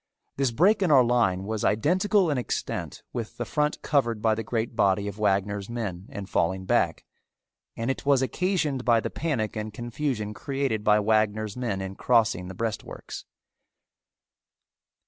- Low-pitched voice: Yes, low, 115 Hz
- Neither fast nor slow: Yes, average, 160 wpm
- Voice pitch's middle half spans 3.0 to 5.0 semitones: Yes, average, 4.4 semitones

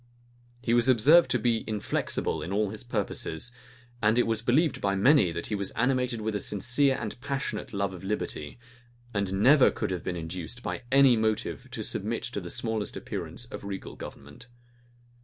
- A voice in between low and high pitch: No, low, 110 Hz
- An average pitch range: Yes, average, 4.1 semitones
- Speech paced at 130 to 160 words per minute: No, average, 180 wpm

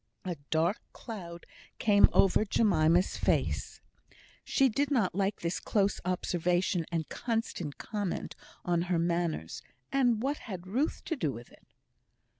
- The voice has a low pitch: No, medium, 185 Hz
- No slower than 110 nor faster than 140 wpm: Yes, slow, 135 wpm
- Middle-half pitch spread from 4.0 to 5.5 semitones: Yes, average, 4.6 semitones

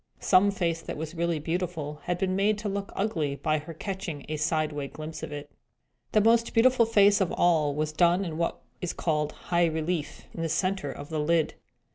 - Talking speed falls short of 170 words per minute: No, average, 200 wpm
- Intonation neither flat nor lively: Yes, average, 3.9 semitones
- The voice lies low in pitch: No, medium, 170 Hz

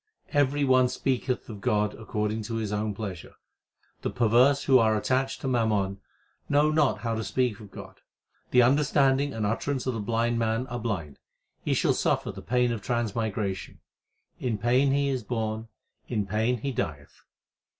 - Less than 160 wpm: No, average, 170 wpm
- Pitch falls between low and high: No, low, 115 Hz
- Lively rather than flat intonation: No, average, 3.4 semitones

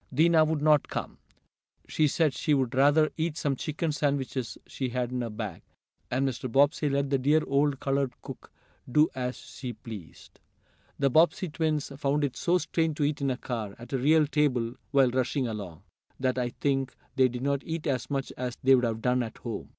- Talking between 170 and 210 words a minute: Yes, average, 200 wpm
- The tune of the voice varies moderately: Yes, average, 3.1 semitones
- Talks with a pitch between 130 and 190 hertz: Yes, low, 135 Hz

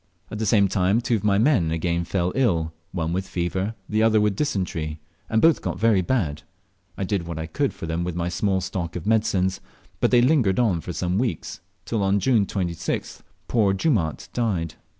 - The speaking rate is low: No, average, 200 wpm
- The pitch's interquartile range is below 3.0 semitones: No, average, 4.3 semitones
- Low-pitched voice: Yes, very low, 95 Hz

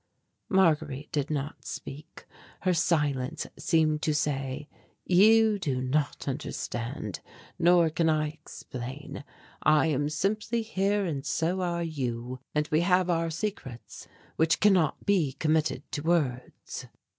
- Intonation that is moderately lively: Yes, average, 3.8 semitones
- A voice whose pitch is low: No, medium, 155 Hz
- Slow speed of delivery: Yes, slow, 125 wpm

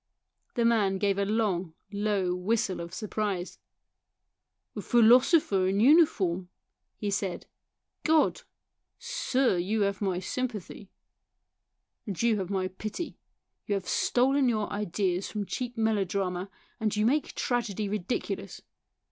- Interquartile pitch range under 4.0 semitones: Yes, average, 3.5 semitones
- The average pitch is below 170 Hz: No, high, 205 Hz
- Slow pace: Yes, slow, 130 wpm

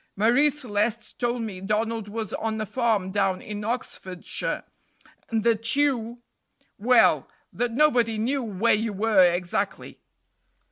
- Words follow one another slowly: Yes, slow, 130 wpm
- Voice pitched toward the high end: Yes, high, 225 Hz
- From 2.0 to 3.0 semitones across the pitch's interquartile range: Yes, narrow, 2.6 semitones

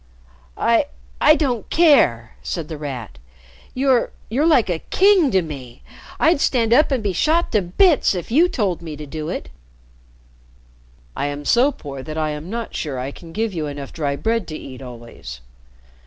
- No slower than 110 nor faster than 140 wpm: No, average, 180 wpm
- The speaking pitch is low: No, medium, 175 Hz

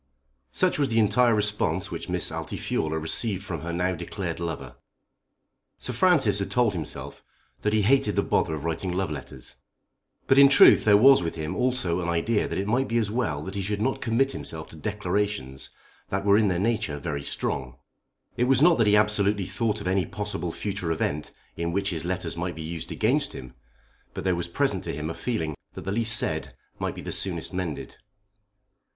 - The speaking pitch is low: Yes, low, 100 Hz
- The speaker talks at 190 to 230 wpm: Yes, average, 200 wpm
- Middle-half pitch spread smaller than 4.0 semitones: No, average, 5.2 semitones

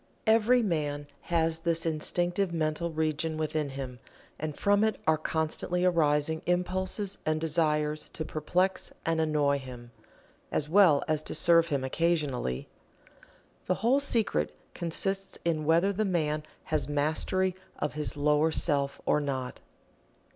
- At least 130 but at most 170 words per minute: Yes, slow, 135 wpm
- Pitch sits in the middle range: Yes, medium, 160 Hz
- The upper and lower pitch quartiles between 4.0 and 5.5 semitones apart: No, average, 3.0 semitones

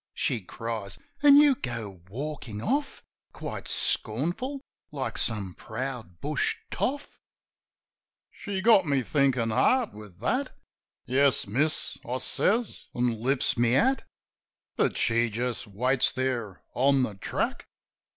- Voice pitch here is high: No, low, 125 Hz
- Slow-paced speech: Yes, slow, 125 wpm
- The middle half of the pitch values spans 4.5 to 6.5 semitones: Yes, wide, 5.5 semitones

